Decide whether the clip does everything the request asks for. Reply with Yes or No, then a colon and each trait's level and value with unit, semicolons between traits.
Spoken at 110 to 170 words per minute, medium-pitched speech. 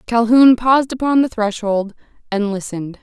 No: average, 140 wpm; high, 230 Hz